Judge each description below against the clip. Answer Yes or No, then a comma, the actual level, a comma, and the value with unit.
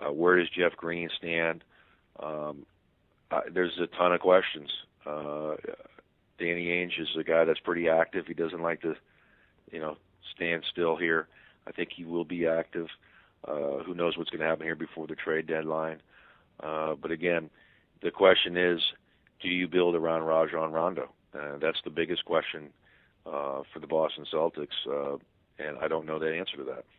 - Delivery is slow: No, average, 180 wpm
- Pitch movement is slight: Yes, narrow, 1.5 semitones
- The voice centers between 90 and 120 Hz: No, very low, 80 Hz